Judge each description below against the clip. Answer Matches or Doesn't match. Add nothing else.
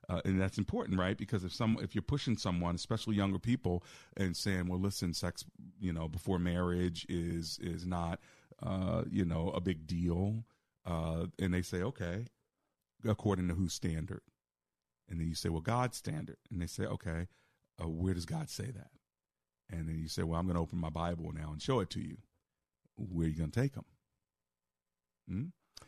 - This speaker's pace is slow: Doesn't match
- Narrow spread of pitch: Doesn't match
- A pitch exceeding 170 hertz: Doesn't match